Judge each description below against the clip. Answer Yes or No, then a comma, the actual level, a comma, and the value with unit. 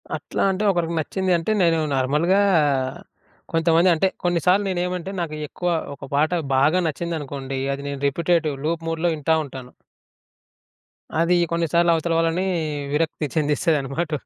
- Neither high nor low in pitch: Yes, medium, 165 Hz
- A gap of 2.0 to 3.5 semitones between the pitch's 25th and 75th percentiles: Yes, average, 2.7 semitones